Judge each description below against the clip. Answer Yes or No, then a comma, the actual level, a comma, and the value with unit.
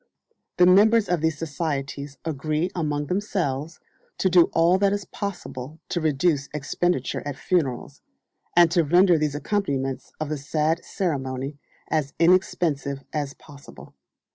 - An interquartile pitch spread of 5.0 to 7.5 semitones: No, average, 4.0 semitones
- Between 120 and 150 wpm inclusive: Yes, slow, 135 wpm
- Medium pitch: Yes, medium, 155 Hz